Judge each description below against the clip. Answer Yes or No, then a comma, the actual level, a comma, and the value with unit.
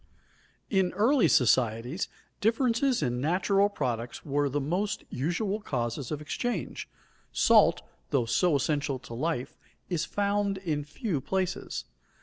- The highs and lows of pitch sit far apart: Yes, wide, 6.9 semitones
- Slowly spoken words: Yes, slow, 125 wpm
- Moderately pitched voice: Yes, medium, 160 Hz